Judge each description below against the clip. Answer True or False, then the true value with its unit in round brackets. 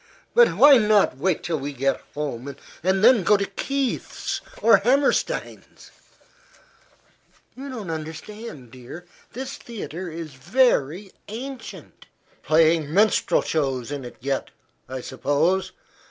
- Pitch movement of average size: False (7.8 semitones)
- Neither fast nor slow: False (120 wpm)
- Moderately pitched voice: True (175 Hz)